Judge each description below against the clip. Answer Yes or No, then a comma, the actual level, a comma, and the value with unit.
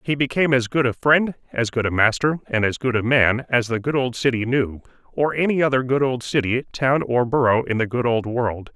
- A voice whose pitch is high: No, low, 125 Hz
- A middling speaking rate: No, fast, 240 wpm